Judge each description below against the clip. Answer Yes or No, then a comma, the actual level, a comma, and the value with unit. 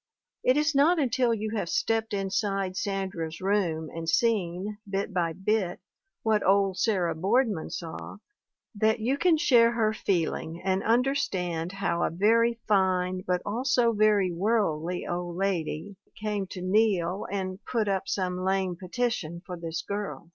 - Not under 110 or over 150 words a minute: Yes, average, 145 wpm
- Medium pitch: No, high, 195 Hz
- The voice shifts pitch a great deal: No, average, 3.6 semitones